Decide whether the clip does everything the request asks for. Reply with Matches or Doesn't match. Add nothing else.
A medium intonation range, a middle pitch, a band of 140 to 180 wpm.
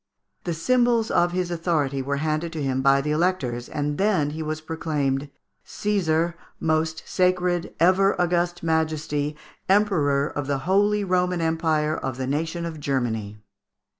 Matches